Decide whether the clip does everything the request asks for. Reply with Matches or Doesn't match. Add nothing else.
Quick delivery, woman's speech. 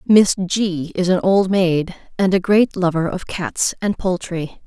Doesn't match